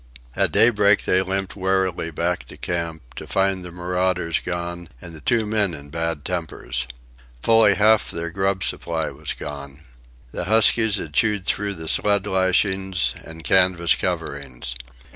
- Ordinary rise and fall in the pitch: Yes, average, 3.0 semitones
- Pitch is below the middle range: Yes, very low, 90 Hz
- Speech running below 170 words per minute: Yes, average, 150 wpm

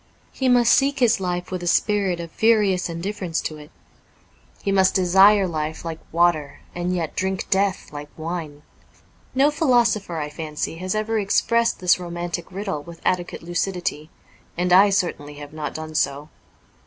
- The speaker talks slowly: No, average, 165 wpm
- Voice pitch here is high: No, medium, 180 Hz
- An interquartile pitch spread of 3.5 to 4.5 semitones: Yes, average, 3.8 semitones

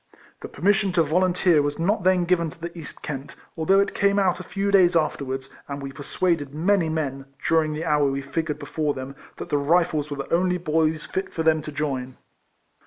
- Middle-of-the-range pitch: Yes, medium, 160 Hz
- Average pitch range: Yes, average, 3.8 semitones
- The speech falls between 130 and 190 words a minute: No, fast, 205 wpm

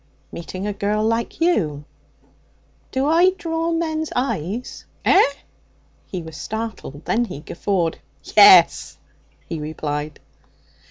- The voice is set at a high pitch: Yes, high, 215 Hz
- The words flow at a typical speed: No, slow, 110 wpm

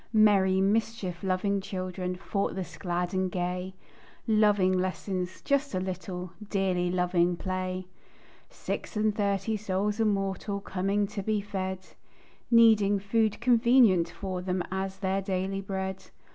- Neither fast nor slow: No, slow, 125 wpm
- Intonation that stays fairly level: Yes, narrow, 1.9 semitones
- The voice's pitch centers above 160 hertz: Yes, high, 190 Hz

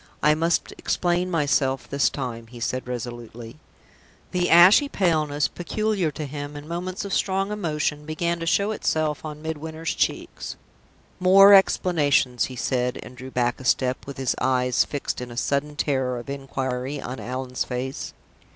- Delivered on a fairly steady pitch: No, average, 4.9 semitones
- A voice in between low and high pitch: Yes, medium, 145 Hz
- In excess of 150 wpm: Yes, average, 160 wpm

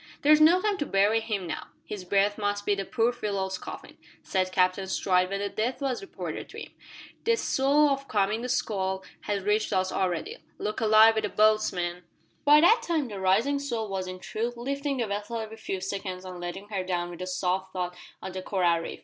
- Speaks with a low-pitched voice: No, high, 205 Hz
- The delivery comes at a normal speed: No, fast, 215 wpm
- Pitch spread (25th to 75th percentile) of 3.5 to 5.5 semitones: Yes, average, 4.2 semitones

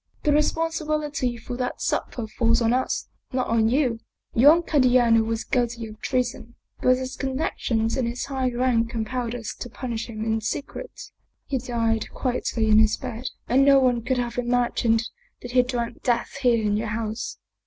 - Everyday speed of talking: Yes, average, 175 wpm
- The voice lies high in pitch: Yes, high, 245 Hz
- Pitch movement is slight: Yes, narrow, 2.1 semitones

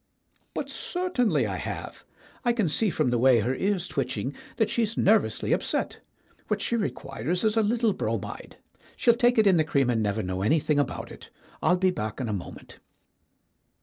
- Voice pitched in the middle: Yes, medium, 175 Hz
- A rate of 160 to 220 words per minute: Yes, average, 180 wpm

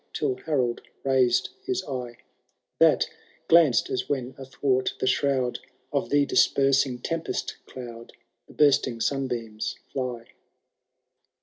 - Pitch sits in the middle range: No, low, 130 Hz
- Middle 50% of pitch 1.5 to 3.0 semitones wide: Yes, narrow, 2.4 semitones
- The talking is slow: Yes, slow, 110 wpm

